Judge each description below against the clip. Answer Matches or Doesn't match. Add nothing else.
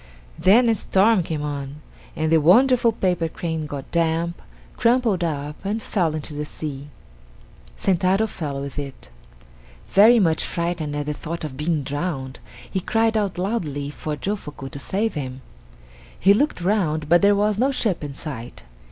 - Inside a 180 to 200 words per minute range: Doesn't match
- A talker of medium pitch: Matches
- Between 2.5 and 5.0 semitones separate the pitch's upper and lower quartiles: Doesn't match